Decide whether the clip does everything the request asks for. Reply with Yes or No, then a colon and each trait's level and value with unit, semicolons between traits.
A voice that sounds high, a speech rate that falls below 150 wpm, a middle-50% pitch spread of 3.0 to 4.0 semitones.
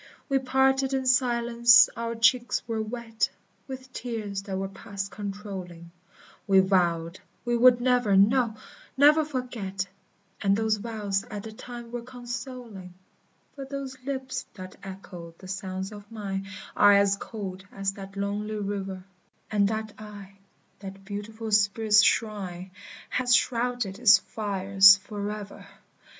Yes: high, 210 Hz; slow, 135 wpm; average, 3.7 semitones